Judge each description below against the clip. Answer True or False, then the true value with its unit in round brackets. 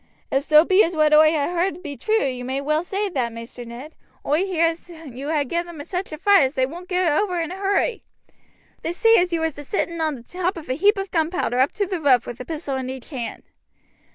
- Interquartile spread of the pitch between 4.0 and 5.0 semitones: True (4.7 semitones)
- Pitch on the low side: False (320 Hz)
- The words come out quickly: True (255 wpm)